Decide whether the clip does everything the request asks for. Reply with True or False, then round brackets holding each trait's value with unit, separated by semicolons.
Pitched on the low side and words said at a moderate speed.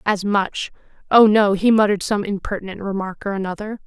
False (200 Hz; 155 wpm)